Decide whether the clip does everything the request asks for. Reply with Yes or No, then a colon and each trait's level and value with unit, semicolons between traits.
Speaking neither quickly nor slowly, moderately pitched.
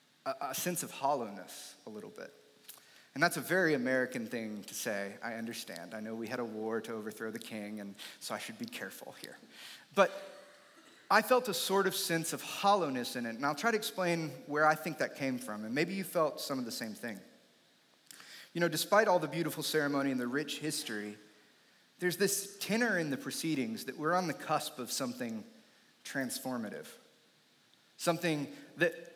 Yes: average, 190 wpm; medium, 155 Hz